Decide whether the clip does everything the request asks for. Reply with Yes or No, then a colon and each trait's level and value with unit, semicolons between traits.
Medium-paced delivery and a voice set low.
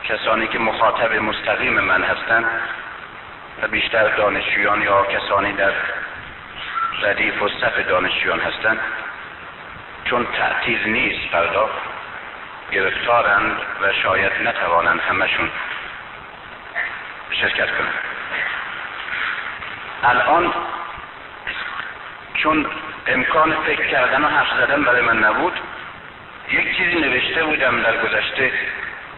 No: slow, 95 wpm; low, 115 Hz